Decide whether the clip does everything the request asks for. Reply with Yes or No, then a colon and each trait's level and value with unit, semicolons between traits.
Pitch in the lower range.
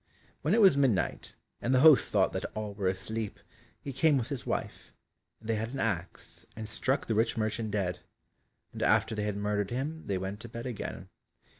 Yes: low, 110 Hz